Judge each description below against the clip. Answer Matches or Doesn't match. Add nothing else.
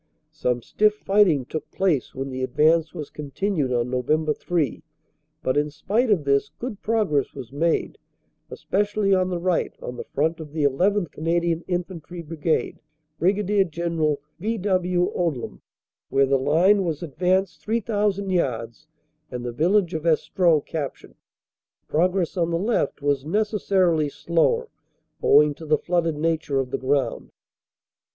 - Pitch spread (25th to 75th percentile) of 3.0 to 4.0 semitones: Doesn't match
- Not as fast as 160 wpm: Matches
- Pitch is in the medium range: Matches